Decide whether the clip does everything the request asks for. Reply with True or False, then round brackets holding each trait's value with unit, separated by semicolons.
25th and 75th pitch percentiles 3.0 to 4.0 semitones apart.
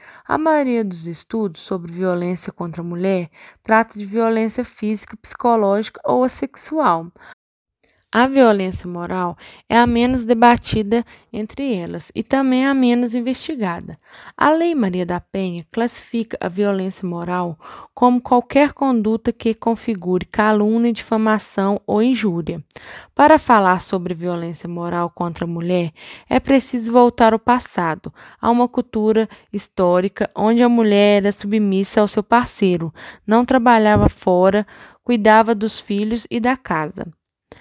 False (4.6 semitones)